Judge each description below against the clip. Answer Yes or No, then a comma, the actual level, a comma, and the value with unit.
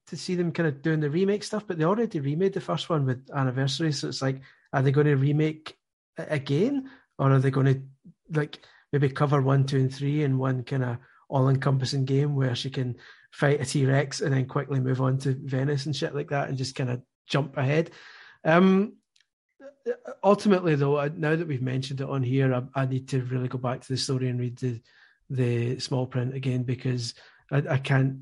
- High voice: No, medium, 140 Hz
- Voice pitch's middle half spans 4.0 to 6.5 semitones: No, average, 2.9 semitones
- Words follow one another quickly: Yes, fast, 215 wpm